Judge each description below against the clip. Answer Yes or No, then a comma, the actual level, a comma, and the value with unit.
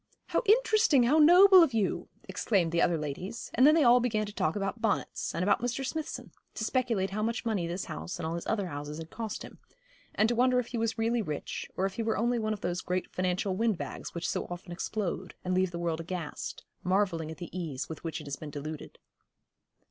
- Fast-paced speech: Yes, fast, 225 wpm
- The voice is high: Yes, high, 195 Hz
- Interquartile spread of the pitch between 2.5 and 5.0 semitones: No, wide, 5.4 semitones